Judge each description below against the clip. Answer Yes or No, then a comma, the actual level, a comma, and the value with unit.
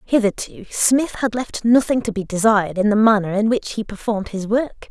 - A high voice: Yes, high, 215 Hz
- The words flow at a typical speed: No, fast, 220 wpm